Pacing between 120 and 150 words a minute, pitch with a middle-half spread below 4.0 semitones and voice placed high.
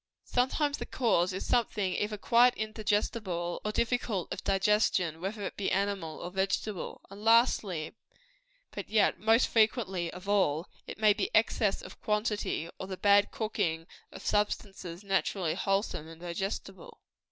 Yes: average, 145 wpm; average, 3.0 semitones; high, 200 Hz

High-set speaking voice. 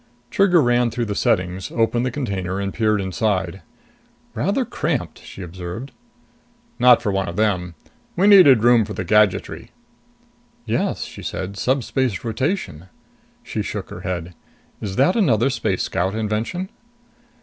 No: low, 110 Hz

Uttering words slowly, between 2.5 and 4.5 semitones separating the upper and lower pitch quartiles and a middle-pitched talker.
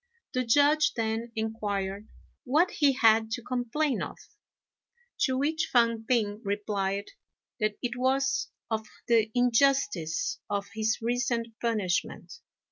No: slow, 120 wpm; average, 3.3 semitones; high, 235 Hz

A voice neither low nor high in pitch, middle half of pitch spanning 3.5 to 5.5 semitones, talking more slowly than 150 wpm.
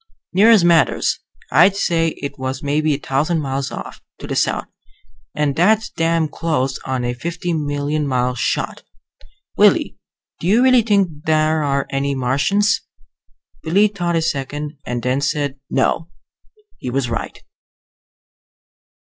Yes: medium, 150 Hz; average, 3.8 semitones; average, 140 wpm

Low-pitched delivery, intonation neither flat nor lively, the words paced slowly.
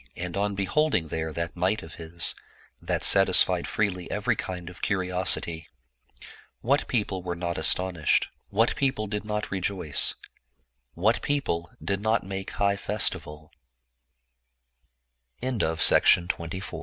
Yes: very low, 95 Hz; average, 3.4 semitones; slow, 120 wpm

